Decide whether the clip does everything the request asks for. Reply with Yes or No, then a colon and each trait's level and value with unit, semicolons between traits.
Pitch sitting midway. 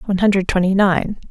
No: high, 195 Hz